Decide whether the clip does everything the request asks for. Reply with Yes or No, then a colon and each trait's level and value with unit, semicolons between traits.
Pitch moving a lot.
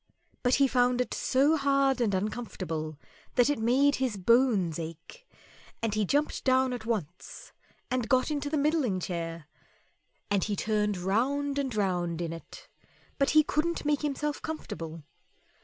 Yes: wide, 6.8 semitones